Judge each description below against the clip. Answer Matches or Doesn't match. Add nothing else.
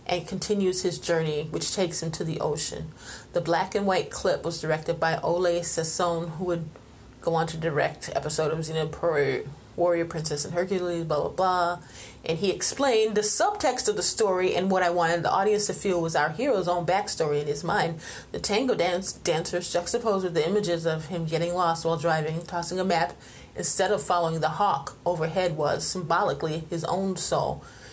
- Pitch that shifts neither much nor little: Doesn't match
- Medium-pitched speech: Matches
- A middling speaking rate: Matches